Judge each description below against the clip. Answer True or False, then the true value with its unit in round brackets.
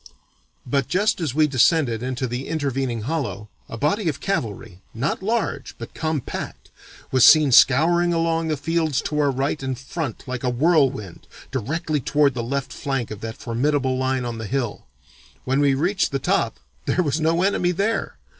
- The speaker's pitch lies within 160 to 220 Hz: False (140 Hz)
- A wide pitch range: False (4.5 semitones)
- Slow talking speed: False (175 wpm)